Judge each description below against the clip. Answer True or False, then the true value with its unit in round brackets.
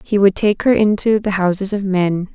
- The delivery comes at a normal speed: False (230 wpm)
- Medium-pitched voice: False (200 Hz)